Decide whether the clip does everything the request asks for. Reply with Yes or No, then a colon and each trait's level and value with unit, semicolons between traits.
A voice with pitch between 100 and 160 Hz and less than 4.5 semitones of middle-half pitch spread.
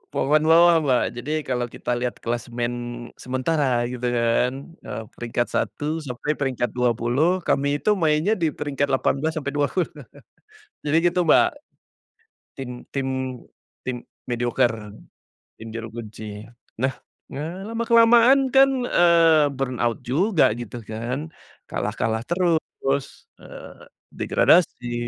No: low, 135 Hz; average, 5.1 semitones